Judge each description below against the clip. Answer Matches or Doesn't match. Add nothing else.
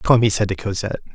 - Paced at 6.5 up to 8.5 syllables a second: Matches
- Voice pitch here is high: Doesn't match